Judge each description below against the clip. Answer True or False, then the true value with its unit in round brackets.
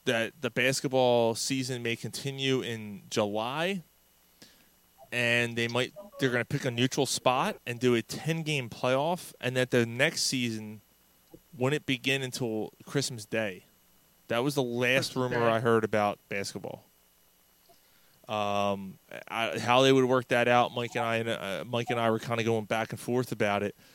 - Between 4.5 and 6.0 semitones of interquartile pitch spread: False (2.7 semitones)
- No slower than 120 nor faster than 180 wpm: True (160 wpm)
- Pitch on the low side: True (120 Hz)